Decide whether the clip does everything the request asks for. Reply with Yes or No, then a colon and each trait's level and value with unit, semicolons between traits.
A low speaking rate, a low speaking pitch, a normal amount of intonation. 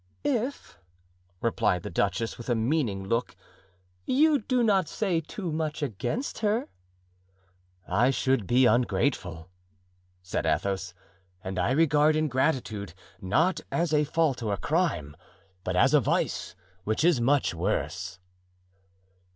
No: slow, 125 wpm; low, 130 Hz; wide, 8.7 semitones